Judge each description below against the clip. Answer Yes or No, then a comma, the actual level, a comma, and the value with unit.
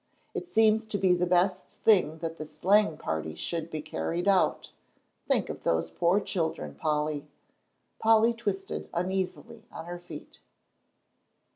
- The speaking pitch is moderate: Yes, medium, 175 Hz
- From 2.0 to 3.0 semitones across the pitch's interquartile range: No, average, 4.4 semitones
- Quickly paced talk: No, average, 140 wpm